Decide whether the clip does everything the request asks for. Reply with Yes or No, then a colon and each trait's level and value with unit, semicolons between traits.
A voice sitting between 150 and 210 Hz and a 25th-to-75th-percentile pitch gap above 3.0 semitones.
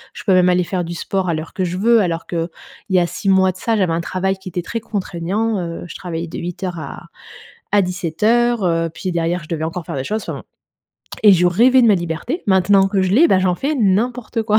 Yes: medium, 185 Hz; average, 3.5 semitones